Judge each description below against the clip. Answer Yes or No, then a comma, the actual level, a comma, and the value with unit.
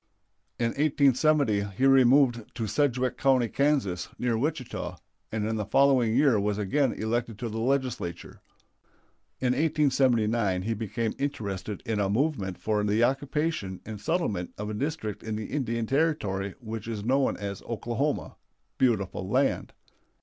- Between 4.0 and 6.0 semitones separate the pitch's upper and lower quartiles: Yes, average, 4.4 semitones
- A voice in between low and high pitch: No, low, 115 Hz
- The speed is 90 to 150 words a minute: Yes, average, 140 wpm